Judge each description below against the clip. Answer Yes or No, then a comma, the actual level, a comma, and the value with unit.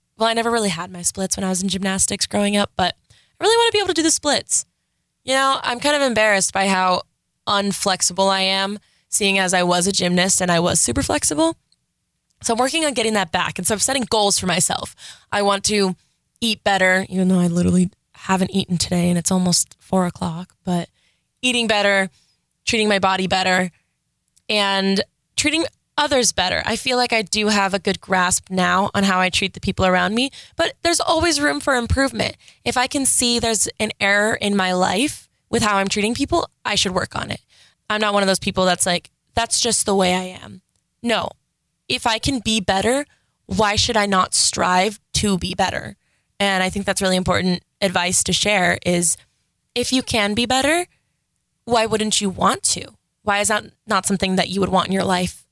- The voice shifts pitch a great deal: No, average, 3.9 semitones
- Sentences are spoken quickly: Yes, fast, 210 wpm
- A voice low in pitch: No, high, 200 Hz